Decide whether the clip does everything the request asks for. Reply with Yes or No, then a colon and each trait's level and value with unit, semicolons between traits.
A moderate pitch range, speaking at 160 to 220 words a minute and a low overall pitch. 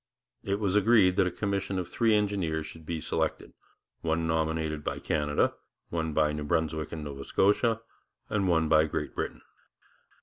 Yes: average, 4.1 semitones; average, 165 wpm; very low, 80 Hz